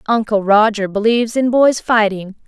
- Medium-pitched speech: No, high, 220 Hz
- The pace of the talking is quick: No, average, 145 wpm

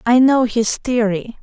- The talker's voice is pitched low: No, high, 235 Hz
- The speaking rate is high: No, average, 170 wpm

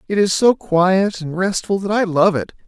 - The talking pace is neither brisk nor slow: No, fast, 225 wpm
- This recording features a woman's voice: No, male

